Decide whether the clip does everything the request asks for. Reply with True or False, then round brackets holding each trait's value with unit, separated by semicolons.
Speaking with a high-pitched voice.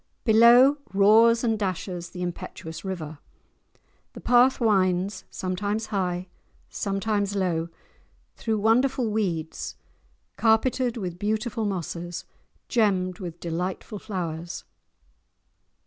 True (200 Hz)